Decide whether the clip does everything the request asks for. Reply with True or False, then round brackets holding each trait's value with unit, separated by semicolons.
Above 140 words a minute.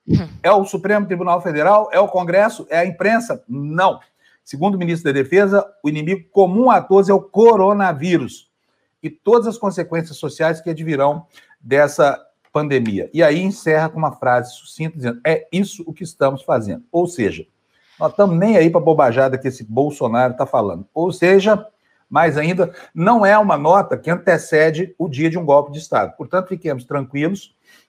True (175 wpm)